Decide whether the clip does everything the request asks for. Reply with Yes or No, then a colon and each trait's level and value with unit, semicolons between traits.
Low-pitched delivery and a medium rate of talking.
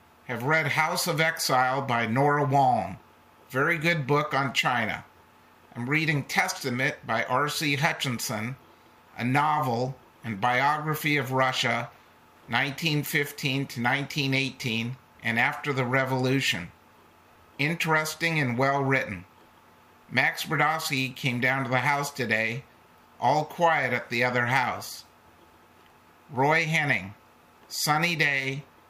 No: low, 130 Hz; slow, 110 wpm